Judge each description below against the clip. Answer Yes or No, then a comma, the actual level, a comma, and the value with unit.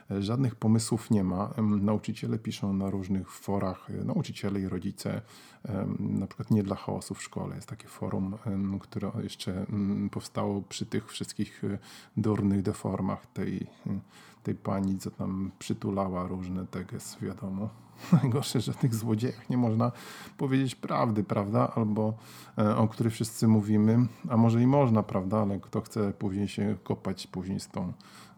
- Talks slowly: No, average, 135 wpm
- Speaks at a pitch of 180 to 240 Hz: No, low, 105 Hz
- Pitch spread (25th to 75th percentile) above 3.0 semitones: No, narrow, 2.5 semitones